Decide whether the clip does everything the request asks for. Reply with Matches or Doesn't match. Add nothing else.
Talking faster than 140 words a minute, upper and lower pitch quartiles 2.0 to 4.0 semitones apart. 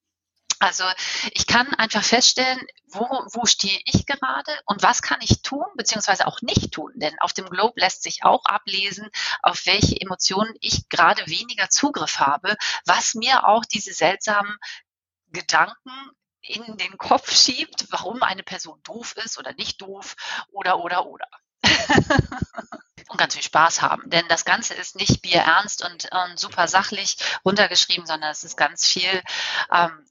Doesn't match